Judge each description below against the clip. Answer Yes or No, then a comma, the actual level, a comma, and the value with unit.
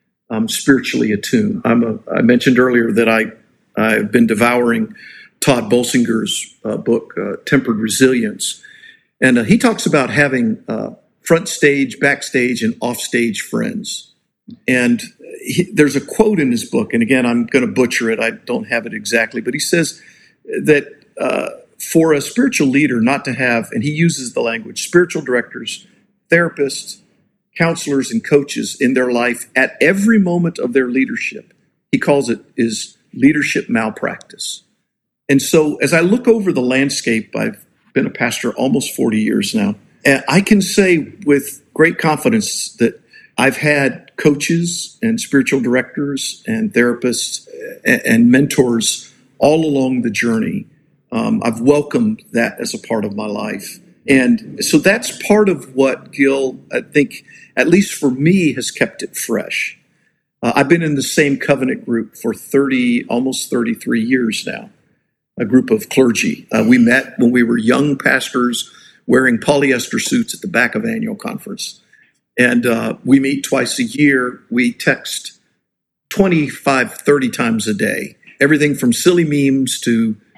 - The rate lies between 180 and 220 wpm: No, average, 160 wpm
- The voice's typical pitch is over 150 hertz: No, medium, 145 Hz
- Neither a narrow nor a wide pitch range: No, wide, 8.9 semitones